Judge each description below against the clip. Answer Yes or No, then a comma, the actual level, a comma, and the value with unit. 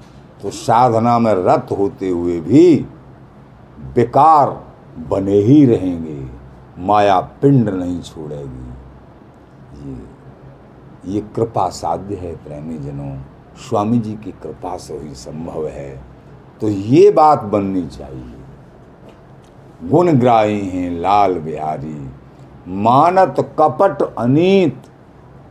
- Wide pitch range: Yes, wide, 7.7 semitones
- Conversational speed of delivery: No, slow, 100 wpm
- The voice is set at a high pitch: No, low, 100 Hz